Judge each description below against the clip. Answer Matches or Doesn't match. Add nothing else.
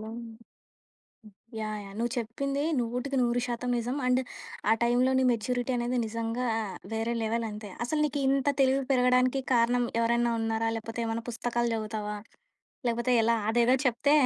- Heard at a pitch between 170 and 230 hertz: Doesn't match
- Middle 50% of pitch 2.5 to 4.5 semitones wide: Doesn't match